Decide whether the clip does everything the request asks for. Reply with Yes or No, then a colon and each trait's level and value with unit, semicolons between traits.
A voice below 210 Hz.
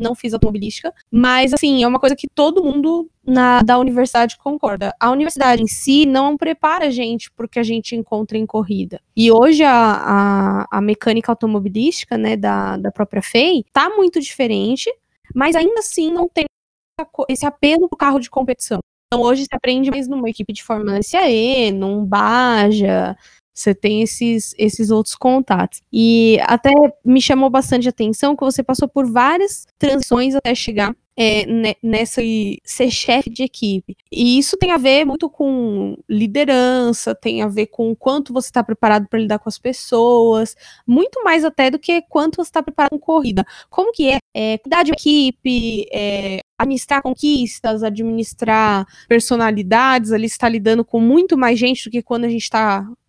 No: high, 245 Hz